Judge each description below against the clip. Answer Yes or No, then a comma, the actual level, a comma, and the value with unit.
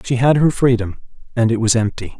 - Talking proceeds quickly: Yes, fast, 220 wpm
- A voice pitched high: No, low, 120 Hz